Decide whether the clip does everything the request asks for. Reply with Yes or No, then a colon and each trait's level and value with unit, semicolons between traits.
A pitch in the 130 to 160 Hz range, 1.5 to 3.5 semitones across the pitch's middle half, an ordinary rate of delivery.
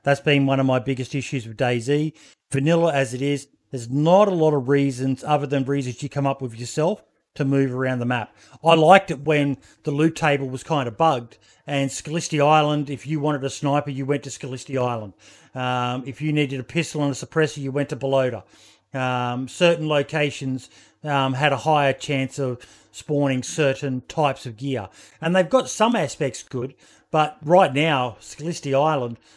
Yes: medium, 140 Hz; narrow, 2.6 semitones; average, 190 wpm